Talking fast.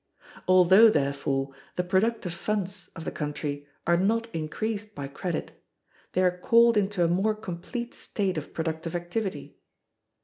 No: average, 140 wpm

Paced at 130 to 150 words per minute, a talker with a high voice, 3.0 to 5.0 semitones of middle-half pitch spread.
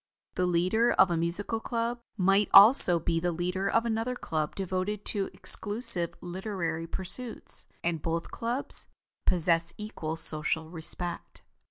No: slow, 135 wpm; medium, 180 Hz; average, 4.2 semitones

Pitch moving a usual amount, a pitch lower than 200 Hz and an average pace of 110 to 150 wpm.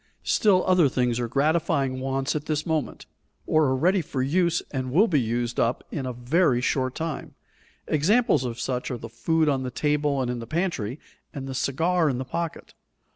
No: average, 4.3 semitones; medium, 140 Hz; average, 195 wpm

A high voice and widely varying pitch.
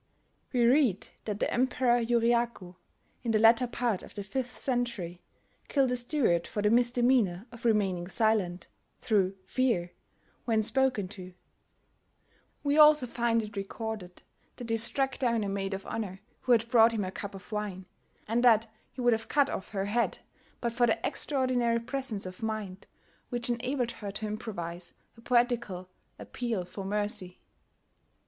No: high, 225 Hz; average, 3.6 semitones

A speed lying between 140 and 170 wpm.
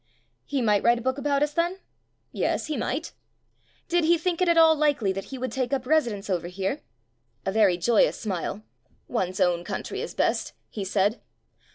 No: average, 195 wpm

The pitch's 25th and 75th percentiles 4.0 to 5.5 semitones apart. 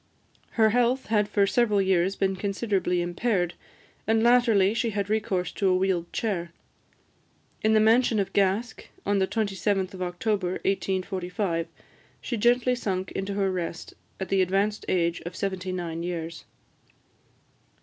No: average, 2.9 semitones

